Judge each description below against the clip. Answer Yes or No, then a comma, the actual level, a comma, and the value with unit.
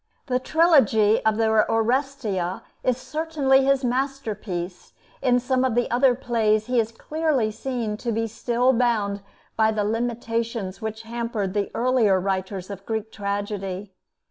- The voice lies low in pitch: No, high, 225 Hz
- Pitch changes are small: No, average, 3.4 semitones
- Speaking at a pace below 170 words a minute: Yes, average, 145 wpm